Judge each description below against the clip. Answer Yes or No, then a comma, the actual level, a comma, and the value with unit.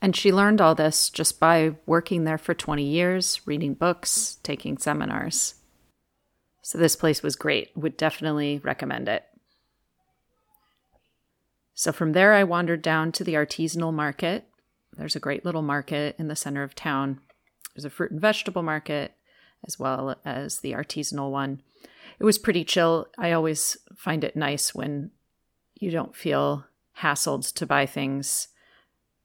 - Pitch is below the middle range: No, medium, 160 Hz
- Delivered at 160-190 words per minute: No, average, 150 wpm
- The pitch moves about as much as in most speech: Yes, average, 3.2 semitones